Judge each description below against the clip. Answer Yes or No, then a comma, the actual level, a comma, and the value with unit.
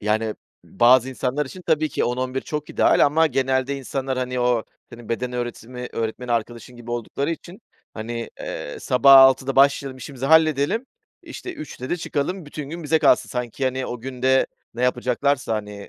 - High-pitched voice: No, low, 130 Hz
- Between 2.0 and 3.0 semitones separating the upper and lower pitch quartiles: Yes, average, 2.7 semitones